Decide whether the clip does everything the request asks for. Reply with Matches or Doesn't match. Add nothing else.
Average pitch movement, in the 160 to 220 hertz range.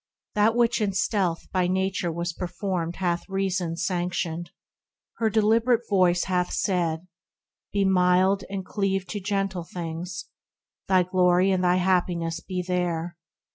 Doesn't match